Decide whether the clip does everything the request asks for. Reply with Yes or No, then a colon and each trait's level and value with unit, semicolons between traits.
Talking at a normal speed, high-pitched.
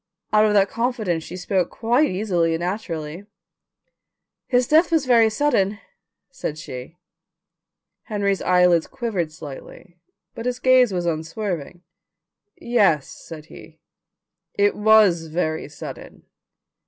No: slow, 115 wpm; high, 195 Hz